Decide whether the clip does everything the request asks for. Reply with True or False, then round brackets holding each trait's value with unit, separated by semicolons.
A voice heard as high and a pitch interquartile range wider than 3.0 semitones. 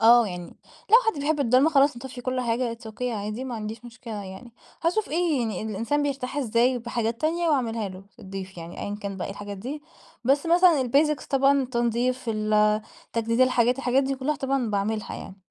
True (240 Hz; 4.2 semitones)